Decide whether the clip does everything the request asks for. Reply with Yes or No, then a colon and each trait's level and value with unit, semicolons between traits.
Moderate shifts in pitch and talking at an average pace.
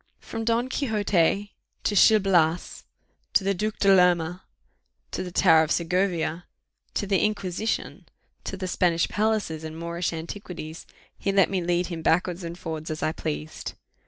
Yes: average, 3.3 semitones; average, 160 wpm